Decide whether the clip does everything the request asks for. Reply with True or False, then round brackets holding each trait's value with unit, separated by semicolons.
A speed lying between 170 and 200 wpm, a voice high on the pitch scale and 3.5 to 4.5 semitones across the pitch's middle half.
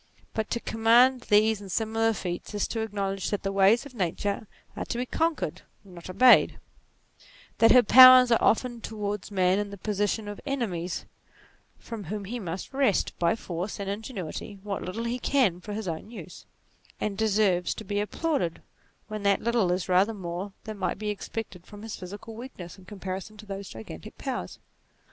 False (185 wpm; 205 Hz; 2.9 semitones)